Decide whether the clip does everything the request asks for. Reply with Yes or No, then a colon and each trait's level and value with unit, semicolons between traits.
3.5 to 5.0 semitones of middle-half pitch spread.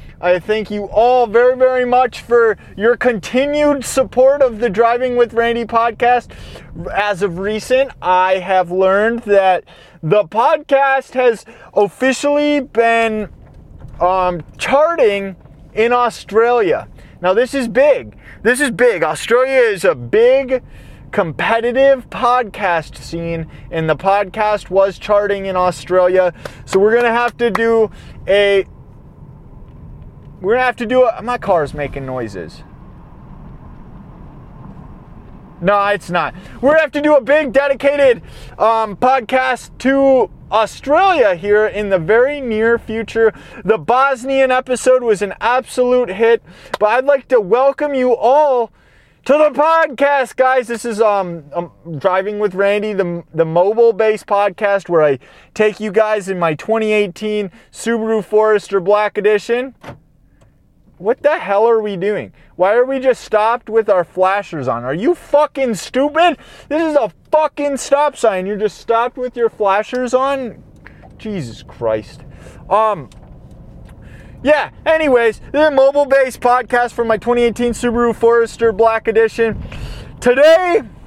Yes: average, 4.5 semitones